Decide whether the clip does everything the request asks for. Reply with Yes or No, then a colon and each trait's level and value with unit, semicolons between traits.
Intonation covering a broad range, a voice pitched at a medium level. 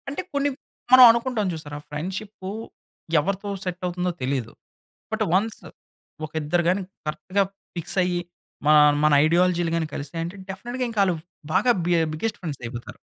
No: average, 4.4 semitones; medium, 180 Hz